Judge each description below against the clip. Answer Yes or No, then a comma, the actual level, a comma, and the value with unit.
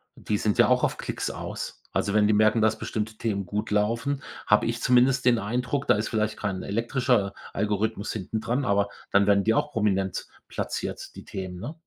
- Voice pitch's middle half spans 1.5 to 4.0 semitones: Yes, narrow, 2.5 semitones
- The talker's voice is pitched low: Yes, low, 110 Hz